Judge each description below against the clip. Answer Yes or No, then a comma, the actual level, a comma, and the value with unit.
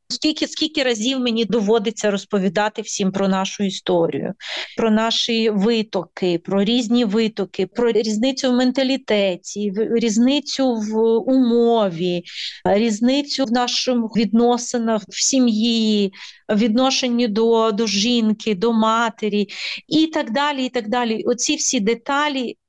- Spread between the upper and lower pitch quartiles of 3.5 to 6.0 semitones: No, average, 2.8 semitones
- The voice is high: Yes, high, 230 Hz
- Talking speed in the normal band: Yes, average, 120 wpm